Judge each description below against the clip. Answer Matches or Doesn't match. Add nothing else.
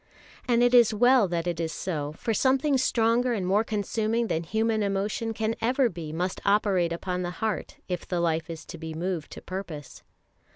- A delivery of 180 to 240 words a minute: Matches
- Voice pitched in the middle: Doesn't match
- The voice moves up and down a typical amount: Matches